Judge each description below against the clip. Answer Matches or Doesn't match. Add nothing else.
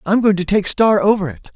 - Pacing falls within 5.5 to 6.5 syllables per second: Matches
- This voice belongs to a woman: Doesn't match